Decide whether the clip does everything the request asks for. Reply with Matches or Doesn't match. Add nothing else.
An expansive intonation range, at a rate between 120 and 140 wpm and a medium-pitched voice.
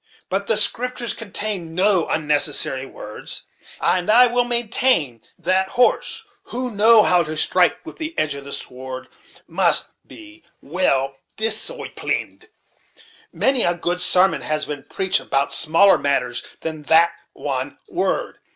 Matches